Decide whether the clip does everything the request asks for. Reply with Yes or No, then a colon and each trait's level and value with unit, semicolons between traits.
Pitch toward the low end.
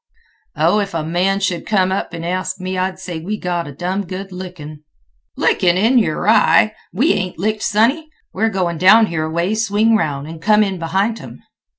No: medium, 185 Hz